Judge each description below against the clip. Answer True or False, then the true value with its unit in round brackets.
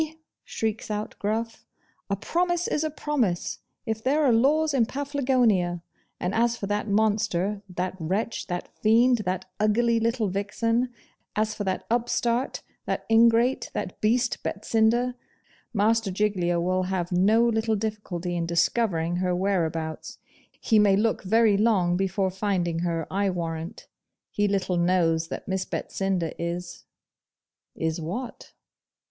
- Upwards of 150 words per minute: False (140 wpm)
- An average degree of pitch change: True (4.2 semitones)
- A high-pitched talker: True (205 Hz)